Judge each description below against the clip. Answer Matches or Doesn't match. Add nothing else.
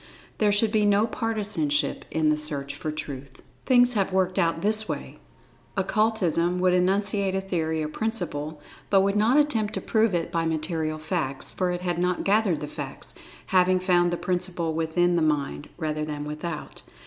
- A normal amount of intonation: Matches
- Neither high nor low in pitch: Matches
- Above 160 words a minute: Matches